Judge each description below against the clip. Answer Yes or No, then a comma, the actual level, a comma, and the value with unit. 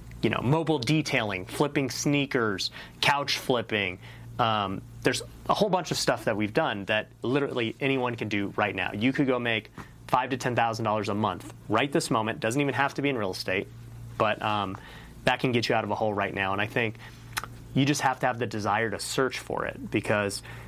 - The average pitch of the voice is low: Yes, low, 120 Hz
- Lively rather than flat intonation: No, average, 3.9 semitones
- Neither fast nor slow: No, fast, 215 wpm